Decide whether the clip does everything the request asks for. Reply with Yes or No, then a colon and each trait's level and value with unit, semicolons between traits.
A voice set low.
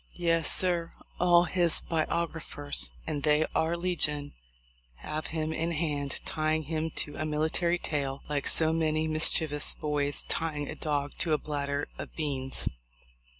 No: medium, 155 Hz